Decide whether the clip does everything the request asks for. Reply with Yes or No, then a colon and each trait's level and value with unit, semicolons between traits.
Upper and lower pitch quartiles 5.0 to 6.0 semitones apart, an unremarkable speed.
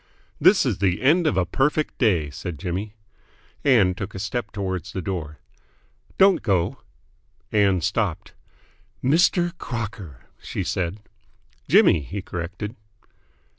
No: wide, 5.6 semitones; slow, 125 wpm